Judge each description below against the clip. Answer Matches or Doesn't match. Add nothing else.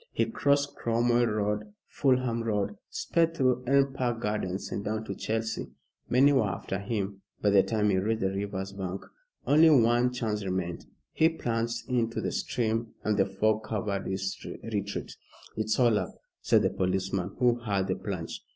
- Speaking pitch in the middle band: Doesn't match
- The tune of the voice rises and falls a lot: Doesn't match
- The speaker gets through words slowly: Doesn't match